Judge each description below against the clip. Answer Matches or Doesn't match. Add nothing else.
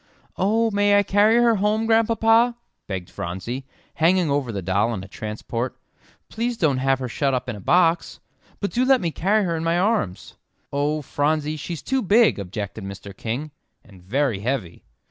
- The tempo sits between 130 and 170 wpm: Doesn't match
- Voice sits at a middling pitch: Matches